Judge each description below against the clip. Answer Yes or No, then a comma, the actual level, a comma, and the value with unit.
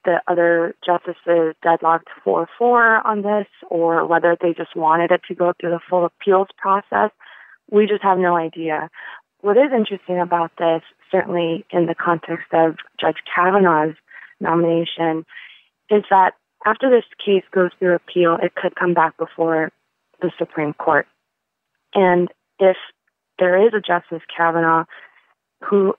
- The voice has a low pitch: No, medium, 175 Hz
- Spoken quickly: No, average, 145 wpm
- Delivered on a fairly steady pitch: Yes, narrow, 2.2 semitones